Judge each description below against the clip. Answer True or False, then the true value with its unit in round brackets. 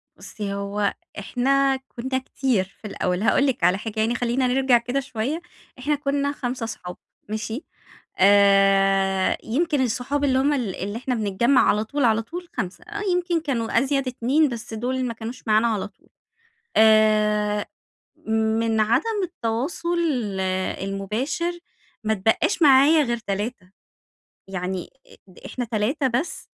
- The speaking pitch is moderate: False (235 Hz)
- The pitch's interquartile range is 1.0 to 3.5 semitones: False (4.3 semitones)